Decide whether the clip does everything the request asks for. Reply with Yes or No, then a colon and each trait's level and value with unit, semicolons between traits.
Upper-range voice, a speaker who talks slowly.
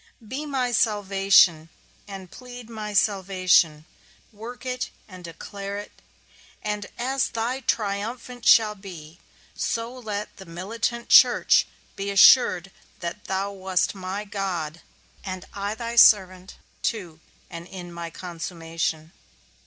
Yes: high, 200 Hz; slow, 120 wpm